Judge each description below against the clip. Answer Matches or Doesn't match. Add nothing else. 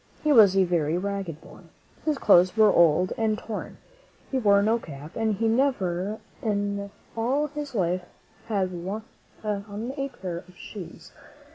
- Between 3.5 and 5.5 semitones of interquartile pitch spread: Matches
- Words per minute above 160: Doesn't match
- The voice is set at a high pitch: Matches